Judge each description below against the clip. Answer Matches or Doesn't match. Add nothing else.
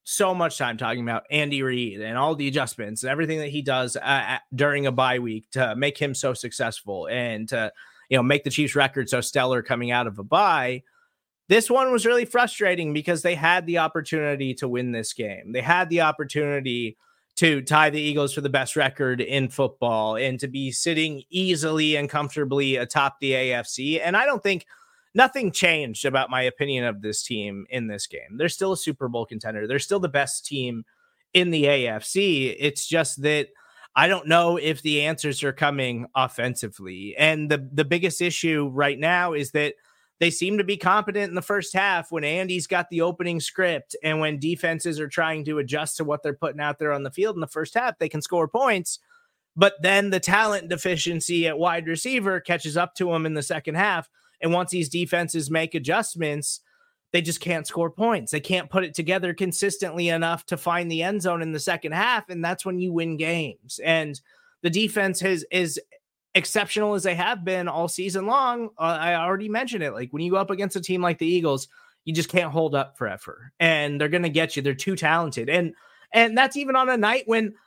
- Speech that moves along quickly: Matches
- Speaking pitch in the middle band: Matches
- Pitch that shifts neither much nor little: Matches